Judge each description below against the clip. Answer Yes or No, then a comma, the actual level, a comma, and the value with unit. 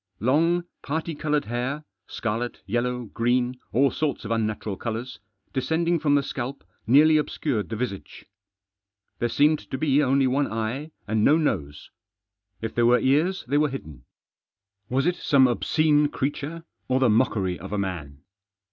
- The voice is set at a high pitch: No, low, 130 Hz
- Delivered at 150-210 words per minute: Yes, average, 160 wpm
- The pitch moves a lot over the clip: No, average, 4.7 semitones